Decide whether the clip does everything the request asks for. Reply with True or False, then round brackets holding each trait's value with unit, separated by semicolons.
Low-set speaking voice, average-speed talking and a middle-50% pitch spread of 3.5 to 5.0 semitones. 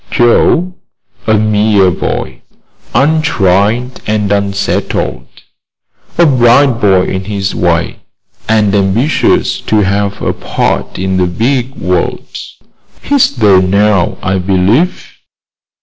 False (105 Hz; 105 wpm; 4.0 semitones)